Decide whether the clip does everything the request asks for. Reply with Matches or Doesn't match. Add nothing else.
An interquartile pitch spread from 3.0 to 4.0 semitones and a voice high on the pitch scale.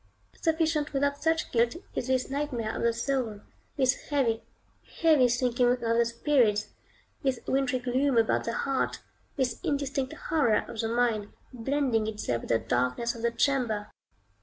Matches